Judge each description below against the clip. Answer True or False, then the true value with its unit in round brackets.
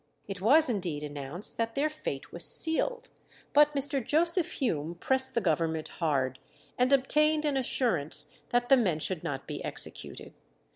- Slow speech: False (155 wpm)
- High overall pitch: True (235 Hz)